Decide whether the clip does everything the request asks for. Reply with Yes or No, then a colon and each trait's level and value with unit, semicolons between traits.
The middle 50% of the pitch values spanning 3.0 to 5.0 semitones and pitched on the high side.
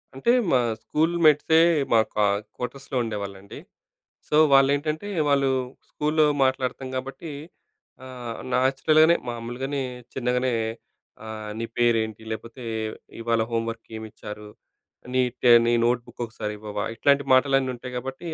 No: average, 3.3 semitones; low, 125 Hz